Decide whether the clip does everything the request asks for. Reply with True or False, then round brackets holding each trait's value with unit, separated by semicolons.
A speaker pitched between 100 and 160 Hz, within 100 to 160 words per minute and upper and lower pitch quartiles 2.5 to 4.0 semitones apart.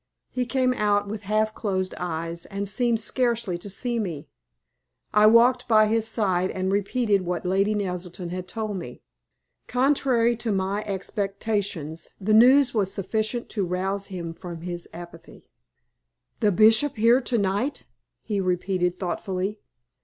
False (200 Hz; 145 wpm; 3.6 semitones)